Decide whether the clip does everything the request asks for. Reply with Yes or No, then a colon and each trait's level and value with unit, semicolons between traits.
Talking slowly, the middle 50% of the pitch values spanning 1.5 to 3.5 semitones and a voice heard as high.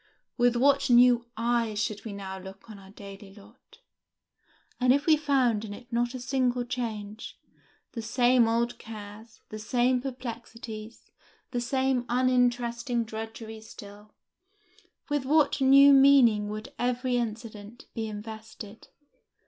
Yes: slow, 130 wpm; narrow, 2.6 semitones; high, 235 Hz